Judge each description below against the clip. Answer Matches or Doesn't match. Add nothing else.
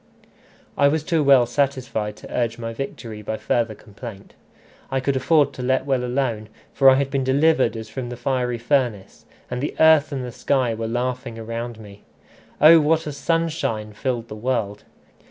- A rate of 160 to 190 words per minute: Matches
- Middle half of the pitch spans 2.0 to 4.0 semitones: Matches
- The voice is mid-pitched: Doesn't match